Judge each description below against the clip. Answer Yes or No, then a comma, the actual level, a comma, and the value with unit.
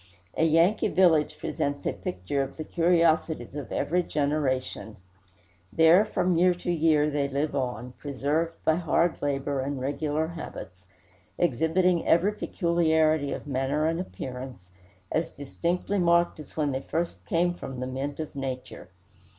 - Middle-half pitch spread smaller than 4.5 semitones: Yes, average, 3.6 semitones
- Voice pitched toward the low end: No, medium, 155 Hz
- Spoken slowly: No, average, 145 wpm